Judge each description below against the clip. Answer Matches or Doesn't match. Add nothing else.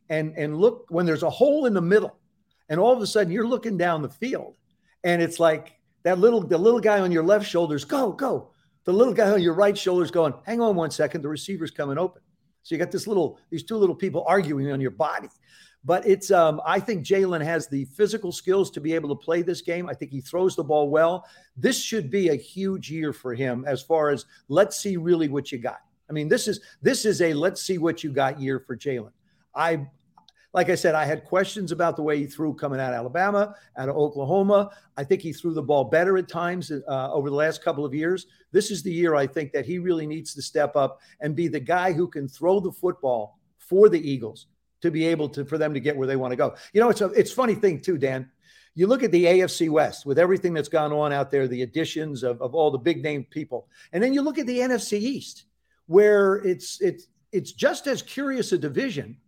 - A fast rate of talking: Matches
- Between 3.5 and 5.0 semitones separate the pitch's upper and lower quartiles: Matches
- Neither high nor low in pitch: Matches